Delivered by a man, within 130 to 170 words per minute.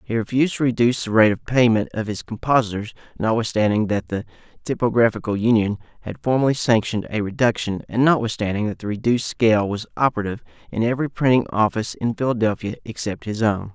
Yes: male; average, 165 wpm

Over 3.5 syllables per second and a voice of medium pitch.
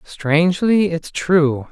No: 3.1 syllables/s; medium, 170 Hz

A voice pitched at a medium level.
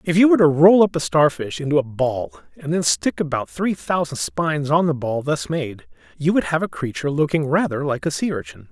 Yes: medium, 150 Hz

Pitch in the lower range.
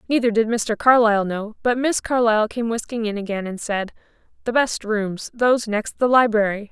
No: high, 225 Hz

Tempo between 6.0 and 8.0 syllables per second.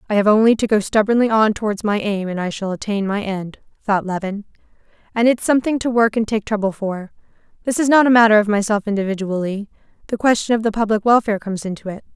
Yes: 6.5 syllables/s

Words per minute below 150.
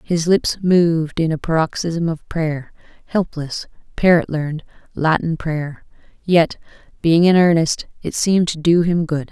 Yes: average, 140 wpm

